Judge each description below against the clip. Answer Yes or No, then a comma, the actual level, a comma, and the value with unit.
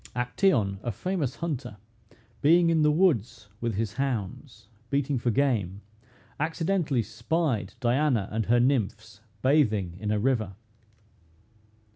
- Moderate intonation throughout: No, wide, 5.7 semitones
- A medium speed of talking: No, slow, 120 wpm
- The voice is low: Yes, low, 120 Hz